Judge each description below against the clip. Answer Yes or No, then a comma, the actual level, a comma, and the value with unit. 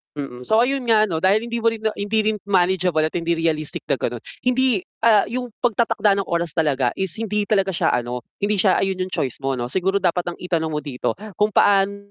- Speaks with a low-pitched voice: No, high, 190 Hz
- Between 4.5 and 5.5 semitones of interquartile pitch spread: Yes, average, 5.1 semitones